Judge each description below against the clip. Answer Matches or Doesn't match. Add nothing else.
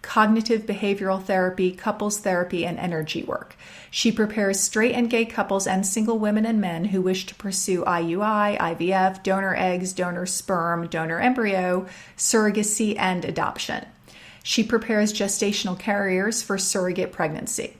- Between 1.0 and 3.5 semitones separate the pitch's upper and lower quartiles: Matches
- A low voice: Doesn't match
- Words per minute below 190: Matches